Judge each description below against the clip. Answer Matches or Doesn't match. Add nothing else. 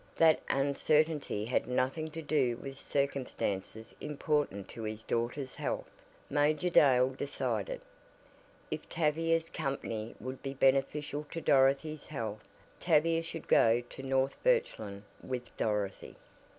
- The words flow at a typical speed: Doesn't match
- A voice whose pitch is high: Doesn't match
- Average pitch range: Matches